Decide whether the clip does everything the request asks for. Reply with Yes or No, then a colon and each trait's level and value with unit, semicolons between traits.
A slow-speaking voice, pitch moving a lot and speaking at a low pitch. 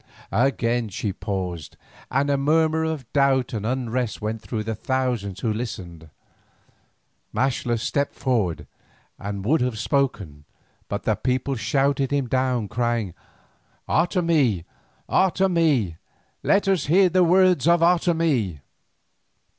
Yes: slow, 120 wpm; wide, 6.3 semitones; low, 130 Hz